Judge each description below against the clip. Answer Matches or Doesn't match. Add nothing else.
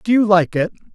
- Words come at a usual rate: Doesn't match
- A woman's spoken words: Doesn't match